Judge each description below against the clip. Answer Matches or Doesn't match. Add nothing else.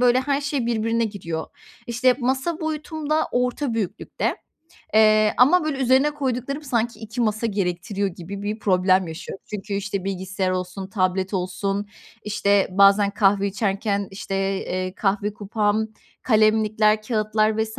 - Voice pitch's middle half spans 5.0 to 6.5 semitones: Doesn't match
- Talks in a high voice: Matches